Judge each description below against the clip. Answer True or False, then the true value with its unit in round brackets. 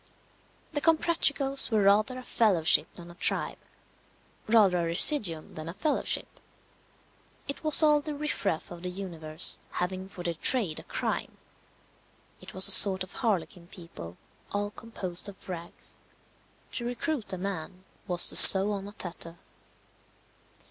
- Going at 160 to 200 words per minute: False (145 wpm)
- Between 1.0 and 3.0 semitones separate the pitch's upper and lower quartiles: False (5.1 semitones)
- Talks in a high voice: True (195 Hz)